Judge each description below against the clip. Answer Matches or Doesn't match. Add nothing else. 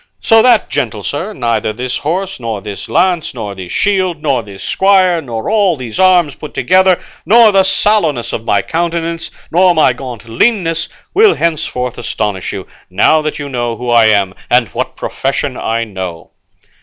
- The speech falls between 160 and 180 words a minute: Matches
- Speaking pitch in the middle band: Matches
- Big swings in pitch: Matches